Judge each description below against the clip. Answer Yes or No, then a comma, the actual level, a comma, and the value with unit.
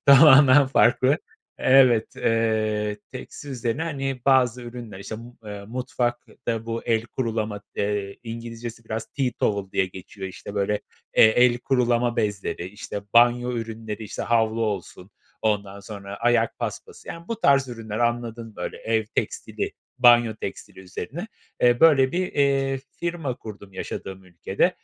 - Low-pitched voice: Yes, low, 115 Hz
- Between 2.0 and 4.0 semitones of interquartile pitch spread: Yes, average, 3.2 semitones